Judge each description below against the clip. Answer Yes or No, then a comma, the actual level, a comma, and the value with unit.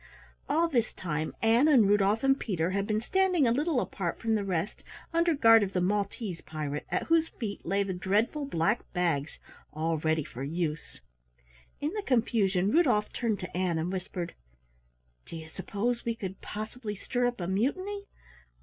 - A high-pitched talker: Yes, high, 205 Hz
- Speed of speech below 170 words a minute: No, average, 175 wpm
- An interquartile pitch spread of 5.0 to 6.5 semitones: Yes, wide, 5.6 semitones